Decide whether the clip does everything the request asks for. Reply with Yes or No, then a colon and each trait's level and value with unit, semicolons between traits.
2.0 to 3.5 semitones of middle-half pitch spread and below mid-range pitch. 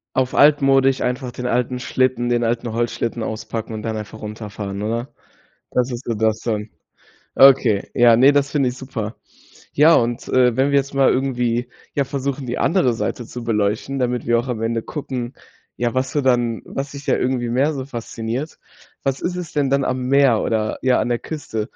Yes: average, 2.8 semitones; low, 125 Hz